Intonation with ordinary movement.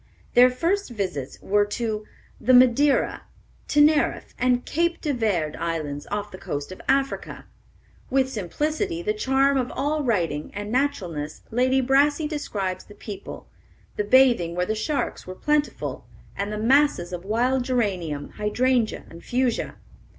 No: wide, 6.0 semitones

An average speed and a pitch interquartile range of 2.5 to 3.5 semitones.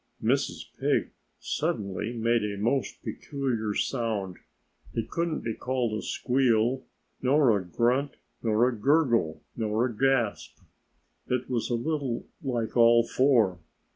No: slow, 130 wpm; average, 3.2 semitones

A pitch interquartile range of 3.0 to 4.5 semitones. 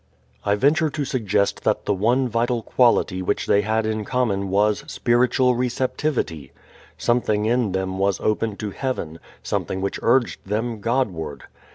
Yes: average, 4.0 semitones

